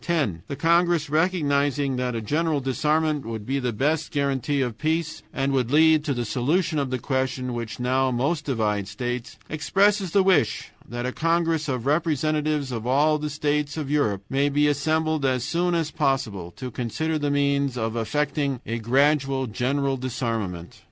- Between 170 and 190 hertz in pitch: No, medium, 140 Hz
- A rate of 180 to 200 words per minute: No, average, 170 wpm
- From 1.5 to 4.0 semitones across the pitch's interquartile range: Yes, average, 3.6 semitones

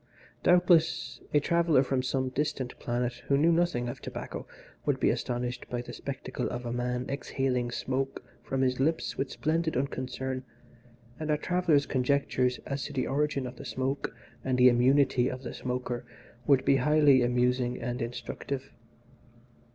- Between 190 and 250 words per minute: No, average, 160 wpm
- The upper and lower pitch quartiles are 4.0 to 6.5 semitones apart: No, narrow, 2.4 semitones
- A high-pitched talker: No, low, 130 Hz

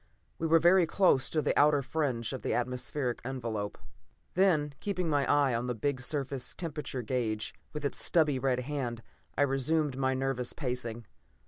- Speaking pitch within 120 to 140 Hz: Yes, low, 135 Hz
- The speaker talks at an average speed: Yes, average, 165 wpm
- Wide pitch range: No, average, 3.4 semitones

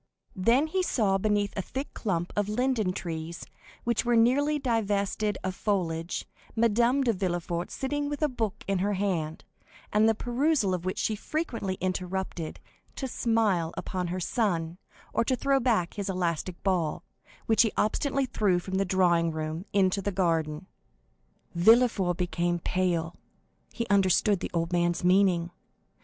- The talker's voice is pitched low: No, high, 195 Hz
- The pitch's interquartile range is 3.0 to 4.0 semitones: No, average, 4.7 semitones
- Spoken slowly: No, average, 150 wpm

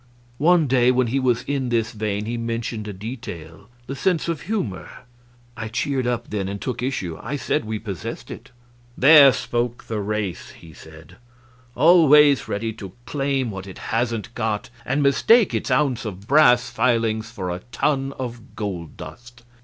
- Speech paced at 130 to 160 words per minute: No, average, 170 wpm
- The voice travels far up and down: No, average, 4.2 semitones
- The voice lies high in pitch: No, low, 120 Hz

